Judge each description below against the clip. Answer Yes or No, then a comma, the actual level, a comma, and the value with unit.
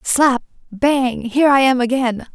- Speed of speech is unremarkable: Yes, average, 155 wpm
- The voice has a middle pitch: No, very high, 255 Hz